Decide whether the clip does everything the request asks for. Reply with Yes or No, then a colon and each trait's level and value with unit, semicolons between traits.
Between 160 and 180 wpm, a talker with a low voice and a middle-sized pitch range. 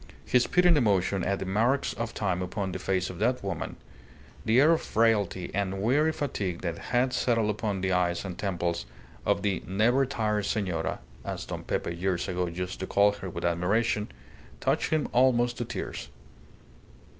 Yes: average, 175 wpm; low, 100 Hz; average, 4.5 semitones